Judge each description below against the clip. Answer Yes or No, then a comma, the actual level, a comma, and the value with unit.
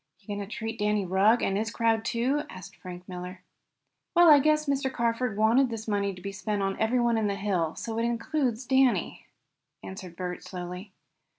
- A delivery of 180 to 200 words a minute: Yes, average, 185 wpm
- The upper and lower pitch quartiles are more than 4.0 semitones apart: No, average, 3.6 semitones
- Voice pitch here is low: No, high, 220 Hz